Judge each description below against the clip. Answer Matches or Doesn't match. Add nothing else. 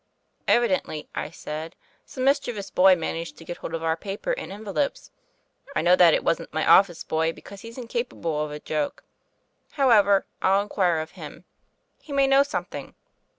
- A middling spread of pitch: Doesn't match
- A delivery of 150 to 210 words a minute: Matches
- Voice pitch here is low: Doesn't match